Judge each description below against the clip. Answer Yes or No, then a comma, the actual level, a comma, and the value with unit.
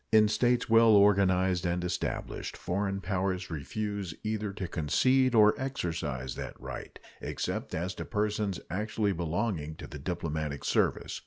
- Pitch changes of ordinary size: Yes, average, 3.8 semitones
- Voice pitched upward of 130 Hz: No, very low, 95 Hz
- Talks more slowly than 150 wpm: Yes, average, 140 wpm